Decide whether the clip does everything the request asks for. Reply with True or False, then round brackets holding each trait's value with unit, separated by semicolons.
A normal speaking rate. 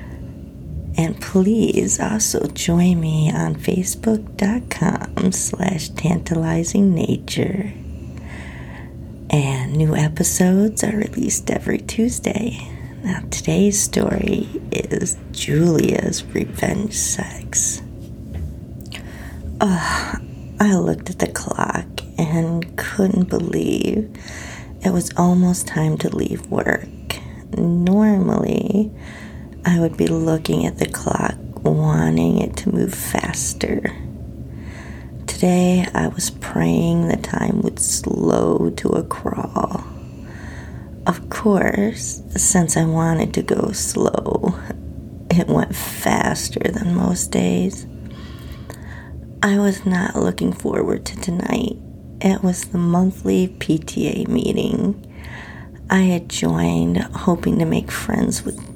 False (100 wpm)